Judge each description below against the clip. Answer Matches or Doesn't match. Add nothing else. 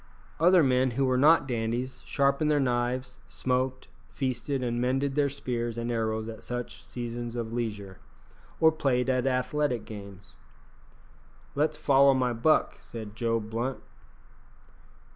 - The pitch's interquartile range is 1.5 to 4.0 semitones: Matches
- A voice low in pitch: Matches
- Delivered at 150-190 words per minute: Doesn't match